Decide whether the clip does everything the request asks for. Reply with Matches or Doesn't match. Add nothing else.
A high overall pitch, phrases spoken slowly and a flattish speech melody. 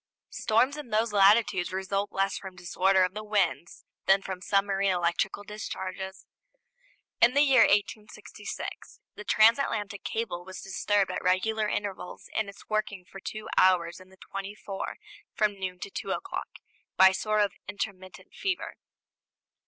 Doesn't match